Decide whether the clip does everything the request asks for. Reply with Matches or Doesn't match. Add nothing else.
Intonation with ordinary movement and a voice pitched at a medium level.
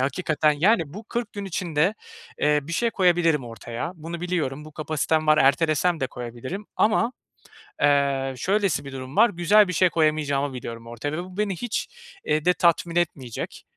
Matches